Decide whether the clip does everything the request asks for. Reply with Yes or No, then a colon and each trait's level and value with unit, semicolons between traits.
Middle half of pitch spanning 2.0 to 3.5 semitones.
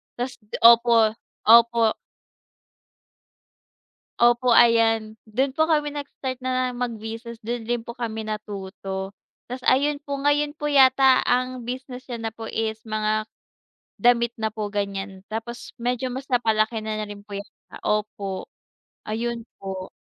Yes: average, 2.7 semitones